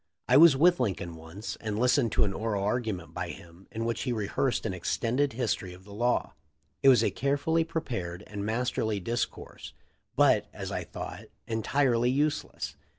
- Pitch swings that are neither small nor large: Yes, average, 4.6 semitones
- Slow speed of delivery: No, average, 175 wpm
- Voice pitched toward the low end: Yes, low, 115 Hz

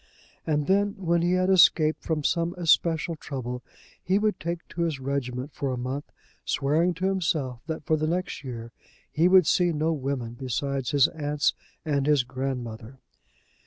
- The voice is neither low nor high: Yes, medium, 150 Hz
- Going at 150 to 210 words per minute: Yes, average, 165 wpm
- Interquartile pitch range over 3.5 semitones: Yes, average, 4.3 semitones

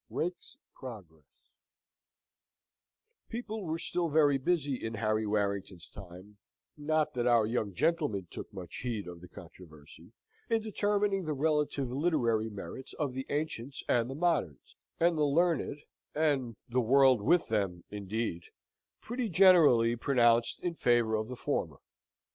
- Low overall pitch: Yes, low, 125 Hz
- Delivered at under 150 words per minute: Yes, slow, 135 wpm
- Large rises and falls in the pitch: Yes, wide, 6.7 semitones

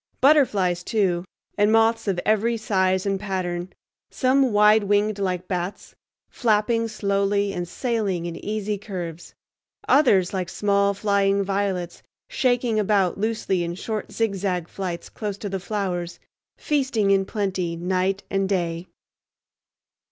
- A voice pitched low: No, high, 200 Hz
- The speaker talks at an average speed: No, slow, 130 wpm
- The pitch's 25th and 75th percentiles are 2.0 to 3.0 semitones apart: Yes, average, 2.7 semitones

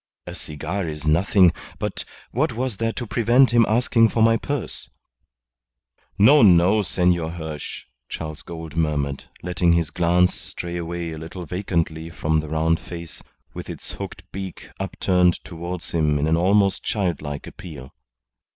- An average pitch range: Yes, average, 3.9 semitones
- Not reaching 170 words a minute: Yes, average, 150 wpm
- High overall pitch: No, very low, 85 Hz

